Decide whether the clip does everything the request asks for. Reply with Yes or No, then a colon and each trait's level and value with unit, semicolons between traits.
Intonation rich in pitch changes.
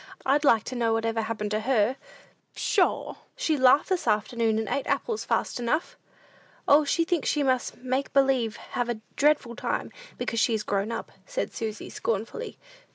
No: average, 4.0 semitones